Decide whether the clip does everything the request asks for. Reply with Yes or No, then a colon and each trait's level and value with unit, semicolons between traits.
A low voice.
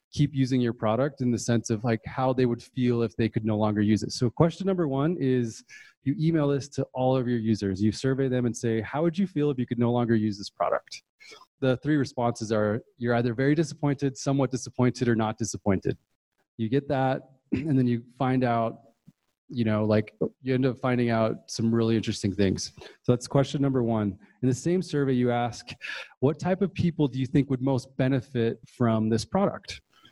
Yes: low, 125 Hz